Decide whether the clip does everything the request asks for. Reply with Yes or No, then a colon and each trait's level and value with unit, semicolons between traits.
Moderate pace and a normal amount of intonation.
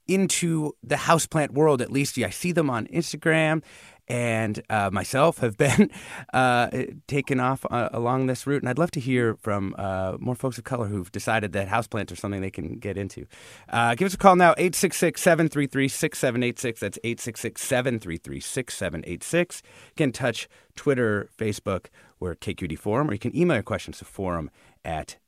No: average, 180 wpm; wide, 6.1 semitones